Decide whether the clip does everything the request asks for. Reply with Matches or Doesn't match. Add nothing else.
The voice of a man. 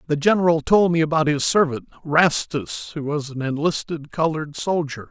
Matches